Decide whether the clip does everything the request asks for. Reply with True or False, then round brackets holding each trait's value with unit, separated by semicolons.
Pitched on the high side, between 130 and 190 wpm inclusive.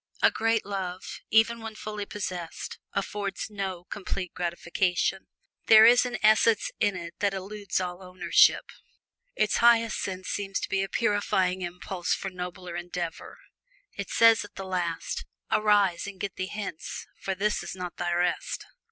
True (195 Hz; 155 wpm)